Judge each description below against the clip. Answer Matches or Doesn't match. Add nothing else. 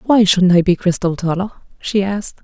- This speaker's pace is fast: Doesn't match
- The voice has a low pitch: Doesn't match